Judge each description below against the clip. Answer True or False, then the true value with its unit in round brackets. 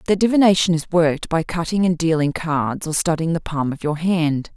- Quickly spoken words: True (210 wpm)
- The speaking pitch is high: False (165 Hz)